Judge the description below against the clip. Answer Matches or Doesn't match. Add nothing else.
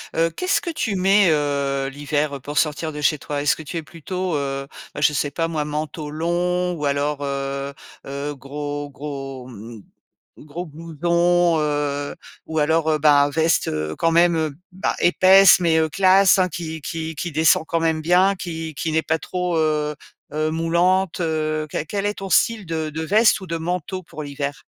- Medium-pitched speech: Matches